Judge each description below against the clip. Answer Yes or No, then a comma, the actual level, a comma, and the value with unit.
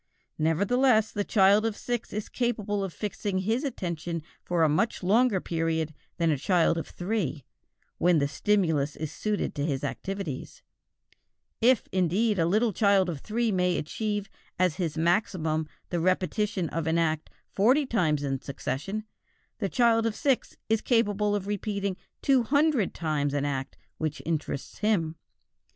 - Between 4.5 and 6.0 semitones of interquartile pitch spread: Yes, average, 5.1 semitones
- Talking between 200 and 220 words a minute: No, average, 155 wpm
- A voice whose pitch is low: No, high, 190 Hz